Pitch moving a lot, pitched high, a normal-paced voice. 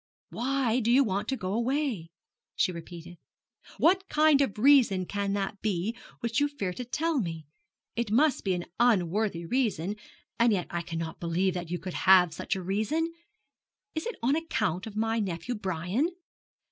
Yes: wide, 6.3 semitones; high, 210 Hz; average, 170 wpm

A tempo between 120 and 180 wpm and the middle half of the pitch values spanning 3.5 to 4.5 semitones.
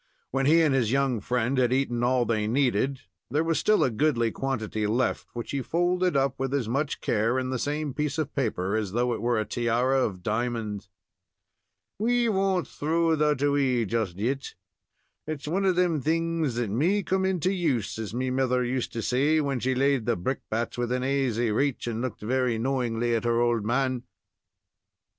No: average, 190 wpm; average, 3.8 semitones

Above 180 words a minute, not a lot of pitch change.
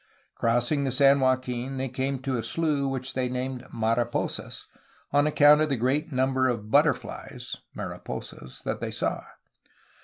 No: average, 155 wpm; narrow, 1.9 semitones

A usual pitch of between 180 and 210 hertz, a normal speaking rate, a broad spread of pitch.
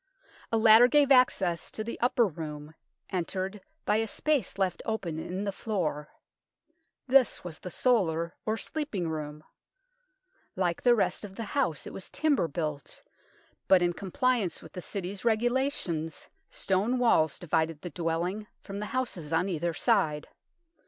Yes: high, 190 Hz; average, 150 wpm; wide, 5.8 semitones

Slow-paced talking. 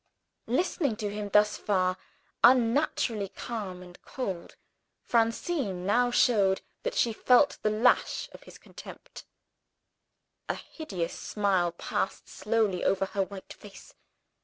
Yes: slow, 120 wpm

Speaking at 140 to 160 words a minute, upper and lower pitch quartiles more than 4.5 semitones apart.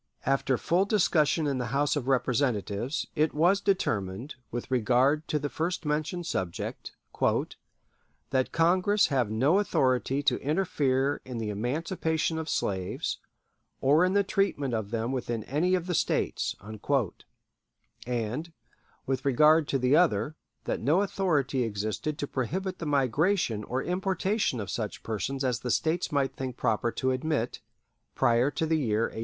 Yes: average, 150 wpm; average, 5.1 semitones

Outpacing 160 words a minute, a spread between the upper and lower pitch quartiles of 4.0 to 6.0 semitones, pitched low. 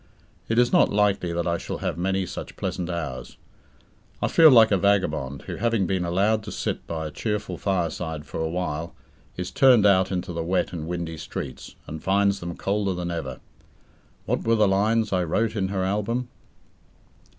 No: average, 185 wpm; average, 3.4 semitones; very low, 95 Hz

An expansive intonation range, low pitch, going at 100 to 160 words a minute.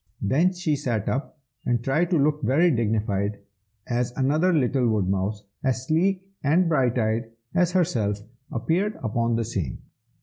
Yes: wide, 6.3 semitones; low, 130 Hz; average, 145 wpm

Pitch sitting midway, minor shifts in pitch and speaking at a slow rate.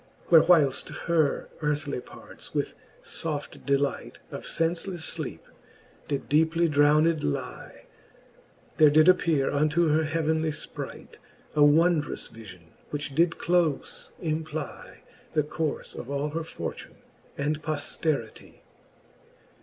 Yes: medium, 155 Hz; narrow, 2.1 semitones; slow, 115 wpm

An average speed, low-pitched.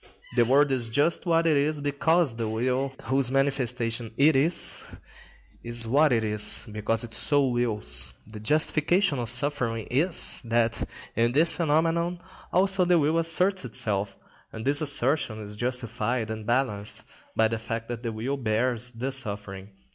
Yes: average, 155 wpm; low, 125 Hz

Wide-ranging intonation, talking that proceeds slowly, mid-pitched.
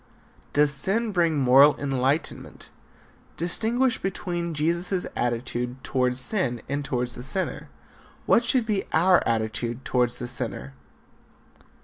Yes: wide, 6.4 semitones; slow, 115 wpm; medium, 145 Hz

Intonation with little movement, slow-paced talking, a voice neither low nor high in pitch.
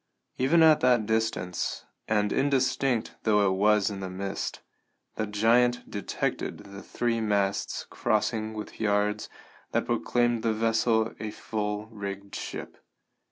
No: narrow, 2.2 semitones; slow, 130 wpm; low, 110 Hz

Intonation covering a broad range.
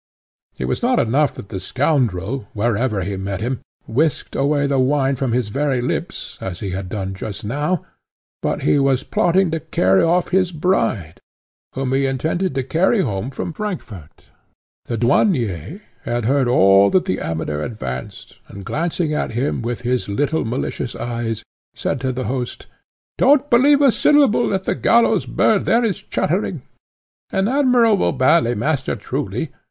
Yes: wide, 7.6 semitones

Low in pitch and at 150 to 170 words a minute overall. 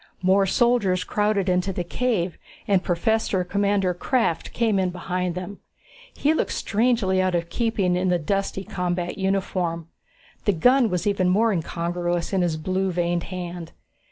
No: medium, 185 Hz; average, 155 wpm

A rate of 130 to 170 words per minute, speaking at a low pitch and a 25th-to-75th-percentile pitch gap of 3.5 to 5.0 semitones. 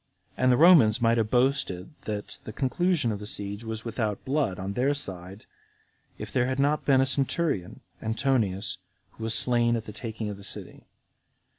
No: average, 180 wpm; low, 115 Hz; average, 4.3 semitones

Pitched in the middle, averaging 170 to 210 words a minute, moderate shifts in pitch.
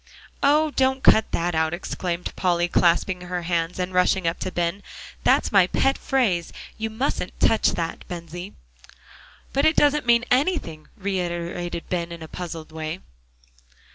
No: medium, 180 Hz; average, 150 wpm; average, 4.7 semitones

